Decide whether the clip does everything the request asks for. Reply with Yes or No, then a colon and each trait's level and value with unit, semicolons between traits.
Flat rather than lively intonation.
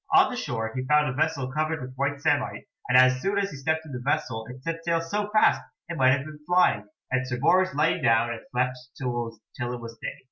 No: average, 4.3 semitones